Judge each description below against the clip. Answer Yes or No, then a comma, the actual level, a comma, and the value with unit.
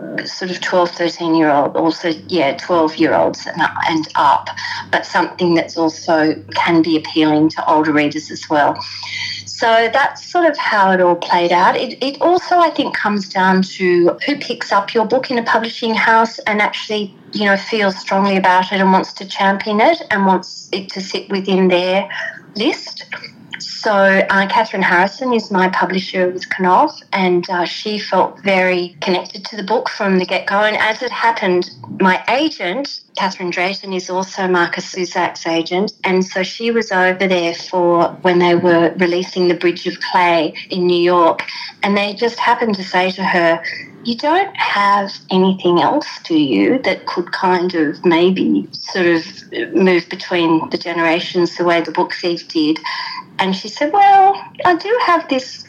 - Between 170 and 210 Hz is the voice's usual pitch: Yes, high, 190 Hz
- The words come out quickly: No, average, 175 wpm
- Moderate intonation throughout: Yes, average, 4.3 semitones